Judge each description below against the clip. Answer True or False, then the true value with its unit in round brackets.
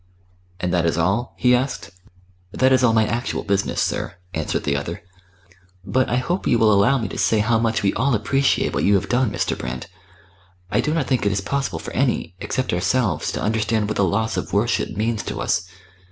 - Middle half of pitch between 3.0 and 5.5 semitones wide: True (4.3 semitones)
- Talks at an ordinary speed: False (210 wpm)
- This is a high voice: False (110 Hz)